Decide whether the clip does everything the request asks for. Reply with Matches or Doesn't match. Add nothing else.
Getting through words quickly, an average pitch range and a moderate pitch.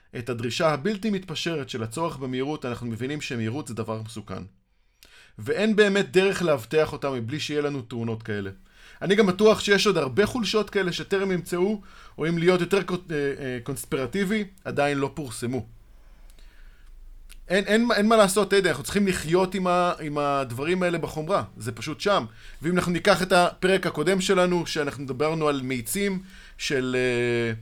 Doesn't match